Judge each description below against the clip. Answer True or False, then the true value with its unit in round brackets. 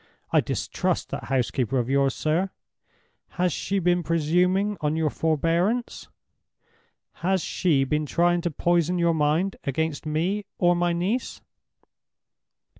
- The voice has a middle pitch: True (170 Hz)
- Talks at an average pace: False (125 wpm)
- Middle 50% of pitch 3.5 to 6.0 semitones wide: False (2.9 semitones)